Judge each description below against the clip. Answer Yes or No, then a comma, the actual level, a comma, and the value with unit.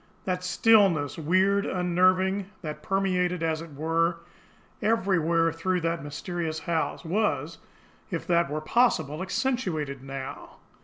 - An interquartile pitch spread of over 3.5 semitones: No, average, 3.0 semitones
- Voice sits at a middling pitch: Yes, medium, 170 Hz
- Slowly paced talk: Yes, slow, 115 wpm